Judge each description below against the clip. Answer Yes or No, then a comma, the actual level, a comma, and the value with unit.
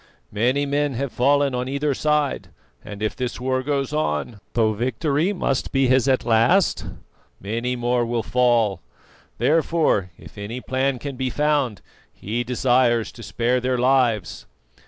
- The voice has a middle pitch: No, low, 125 Hz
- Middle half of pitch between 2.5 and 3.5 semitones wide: Yes, average, 3.1 semitones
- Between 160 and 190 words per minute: No, average, 150 wpm